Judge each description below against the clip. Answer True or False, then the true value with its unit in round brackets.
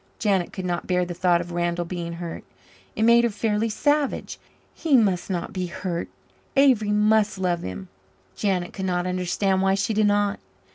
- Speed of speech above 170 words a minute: True (180 wpm)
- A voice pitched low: False (190 Hz)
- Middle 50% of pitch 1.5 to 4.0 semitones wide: True (3.2 semitones)